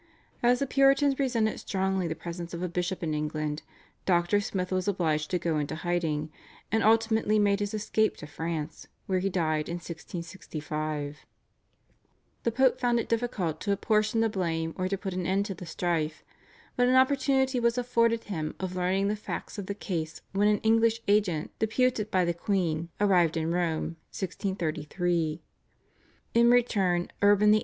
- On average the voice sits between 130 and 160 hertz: No, high, 190 Hz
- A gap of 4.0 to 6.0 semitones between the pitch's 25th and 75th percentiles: Yes, average, 4.7 semitones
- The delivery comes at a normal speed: Yes, average, 170 wpm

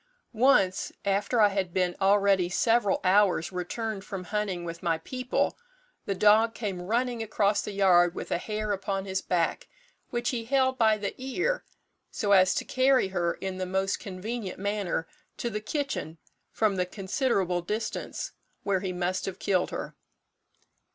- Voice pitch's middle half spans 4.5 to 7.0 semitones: No, average, 3.3 semitones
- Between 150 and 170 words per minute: Yes, average, 160 wpm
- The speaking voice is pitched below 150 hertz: No, high, 200 Hz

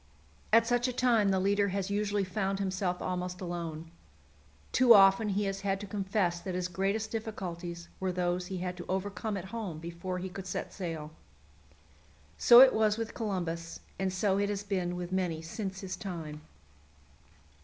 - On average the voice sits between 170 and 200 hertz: Yes, high, 190 Hz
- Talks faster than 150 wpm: Yes, average, 175 wpm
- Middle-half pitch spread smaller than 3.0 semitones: Yes, narrow, 2.4 semitones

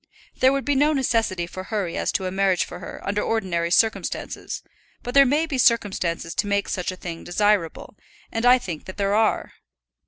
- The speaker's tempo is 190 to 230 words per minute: Yes, average, 195 wpm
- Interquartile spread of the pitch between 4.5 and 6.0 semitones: Yes, average, 5.1 semitones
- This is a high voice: Yes, high, 205 Hz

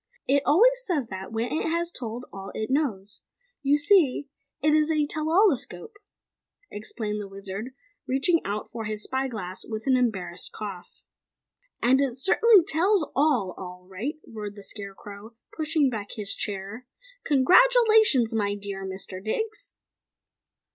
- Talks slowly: No, average, 145 wpm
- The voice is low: No, high, 245 Hz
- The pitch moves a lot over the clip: Yes, wide, 7.2 semitones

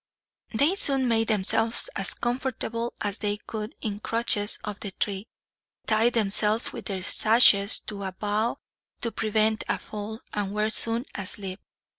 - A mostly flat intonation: Yes, narrow, 2.1 semitones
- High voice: Yes, high, 215 Hz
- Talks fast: No, average, 150 wpm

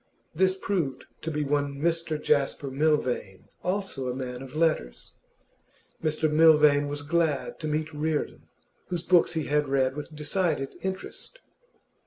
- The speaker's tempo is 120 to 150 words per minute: Yes, average, 140 wpm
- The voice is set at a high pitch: No, medium, 150 Hz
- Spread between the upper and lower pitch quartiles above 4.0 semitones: No, average, 2.7 semitones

